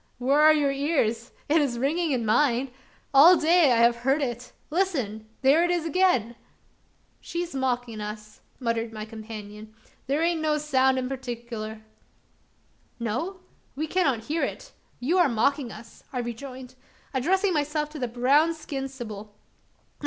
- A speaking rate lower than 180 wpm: Yes, average, 150 wpm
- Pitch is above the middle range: Yes, very high, 265 Hz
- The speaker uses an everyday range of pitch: Yes, average, 4.8 semitones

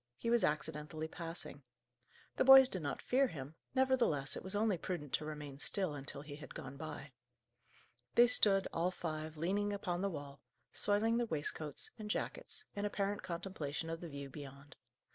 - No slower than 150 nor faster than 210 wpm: Yes, average, 170 wpm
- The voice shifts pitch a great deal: Yes, wide, 5.7 semitones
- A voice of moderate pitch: Yes, medium, 165 Hz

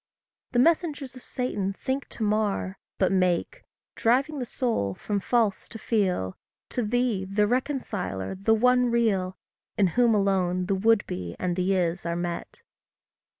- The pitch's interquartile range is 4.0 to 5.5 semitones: Yes, average, 4.9 semitones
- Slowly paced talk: No, average, 150 wpm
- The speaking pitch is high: Yes, high, 205 Hz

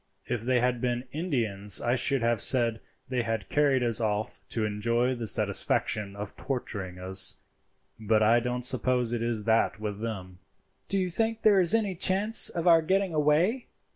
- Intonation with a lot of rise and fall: Yes, wide, 5.8 semitones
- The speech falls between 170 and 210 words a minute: Yes, average, 175 wpm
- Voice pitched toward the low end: Yes, low, 120 Hz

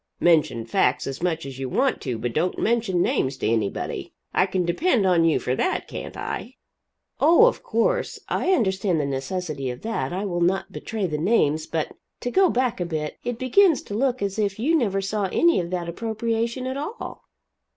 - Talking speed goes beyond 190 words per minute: Yes, average, 200 wpm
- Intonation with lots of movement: Yes, wide, 7.3 semitones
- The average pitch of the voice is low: No, high, 190 Hz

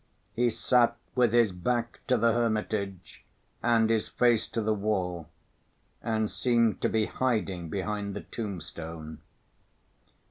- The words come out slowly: Yes, slow, 130 wpm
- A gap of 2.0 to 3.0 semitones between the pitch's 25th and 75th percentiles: No, average, 3.5 semitones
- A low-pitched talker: Yes, low, 110 Hz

